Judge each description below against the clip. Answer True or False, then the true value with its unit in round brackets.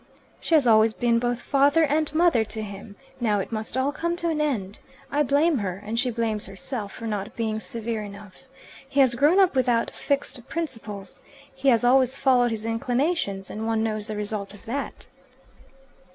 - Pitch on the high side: True (235 Hz)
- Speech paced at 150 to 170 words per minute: False (185 wpm)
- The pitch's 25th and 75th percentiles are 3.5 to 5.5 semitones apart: True (4.5 semitones)